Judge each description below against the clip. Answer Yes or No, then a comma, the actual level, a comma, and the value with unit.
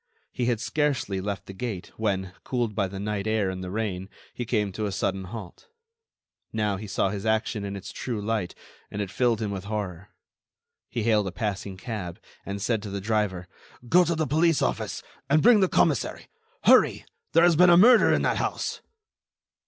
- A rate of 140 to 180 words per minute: No, average, 195 wpm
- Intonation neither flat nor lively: Yes, average, 3.6 semitones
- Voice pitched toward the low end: Yes, low, 105 Hz